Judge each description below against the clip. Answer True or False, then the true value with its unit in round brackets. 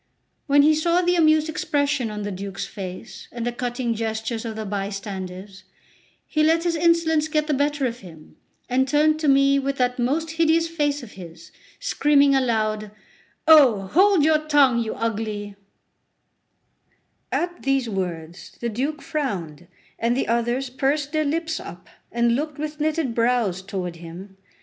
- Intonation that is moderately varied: False (6.4 semitones)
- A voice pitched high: True (255 Hz)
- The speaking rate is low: False (160 wpm)